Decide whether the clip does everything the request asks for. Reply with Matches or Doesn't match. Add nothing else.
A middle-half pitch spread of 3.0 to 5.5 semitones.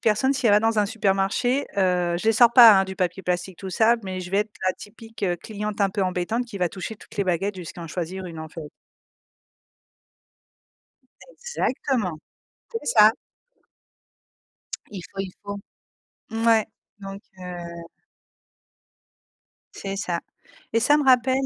Matches